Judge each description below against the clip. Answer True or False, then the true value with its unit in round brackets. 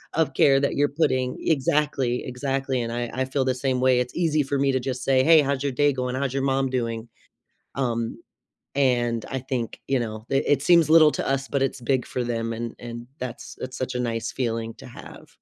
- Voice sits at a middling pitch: False (130 Hz)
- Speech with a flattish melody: True (2.3 semitones)